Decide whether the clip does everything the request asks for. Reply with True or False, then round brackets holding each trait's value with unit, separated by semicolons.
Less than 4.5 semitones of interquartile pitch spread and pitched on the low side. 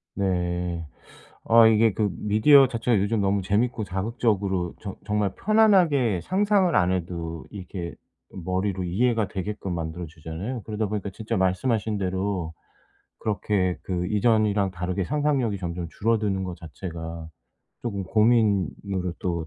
True (3.8 semitones; 100 Hz)